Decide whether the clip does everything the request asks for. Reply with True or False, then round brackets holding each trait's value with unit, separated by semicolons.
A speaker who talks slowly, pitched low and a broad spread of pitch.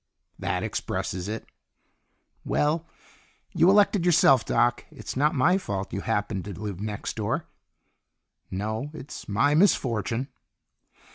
True (120 wpm; 120 Hz; 7.2 semitones)